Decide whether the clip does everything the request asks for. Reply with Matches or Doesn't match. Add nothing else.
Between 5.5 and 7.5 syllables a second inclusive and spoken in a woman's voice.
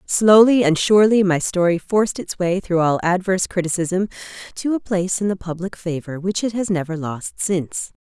Doesn't match